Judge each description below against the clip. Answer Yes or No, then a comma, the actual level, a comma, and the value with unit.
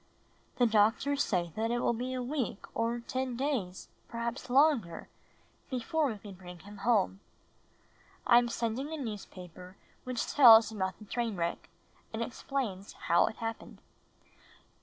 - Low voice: No, high, 230 Hz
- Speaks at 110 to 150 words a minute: Yes, average, 145 wpm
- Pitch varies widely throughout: No, average, 4.2 semitones